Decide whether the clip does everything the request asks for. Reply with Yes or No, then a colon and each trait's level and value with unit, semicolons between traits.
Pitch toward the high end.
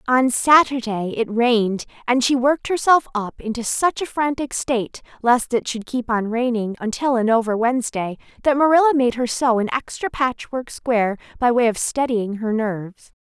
Yes: high, 240 Hz